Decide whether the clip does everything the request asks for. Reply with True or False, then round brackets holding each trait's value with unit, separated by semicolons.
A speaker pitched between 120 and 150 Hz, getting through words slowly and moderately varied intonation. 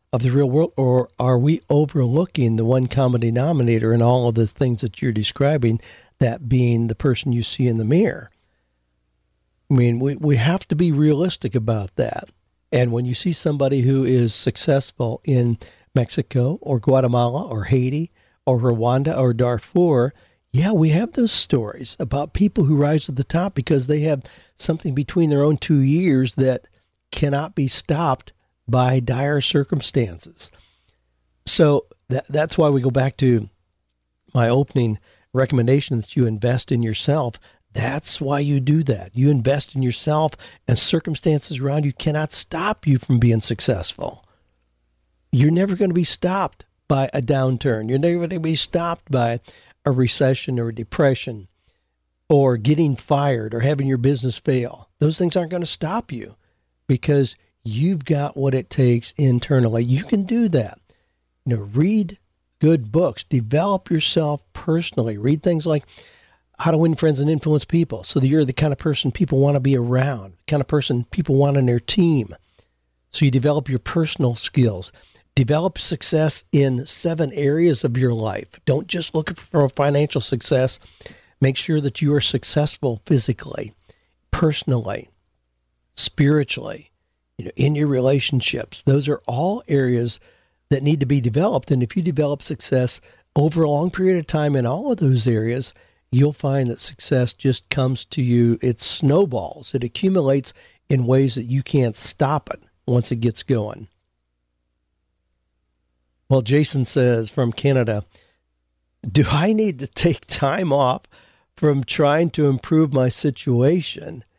False (135 Hz; 160 wpm; 4.1 semitones)